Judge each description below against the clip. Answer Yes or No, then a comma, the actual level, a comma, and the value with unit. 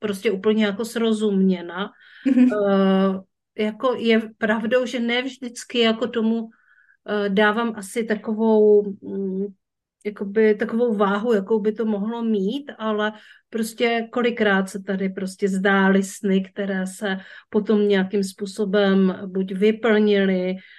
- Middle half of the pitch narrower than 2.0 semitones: No, narrow, 2.4 semitones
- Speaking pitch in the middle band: No, high, 210 Hz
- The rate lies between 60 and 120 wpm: Yes, slow, 115 wpm